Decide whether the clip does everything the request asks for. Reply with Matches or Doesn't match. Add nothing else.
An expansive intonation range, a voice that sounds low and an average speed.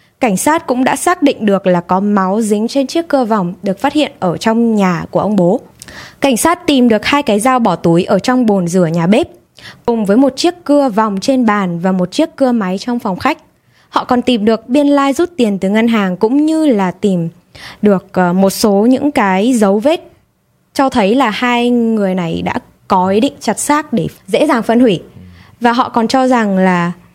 Doesn't match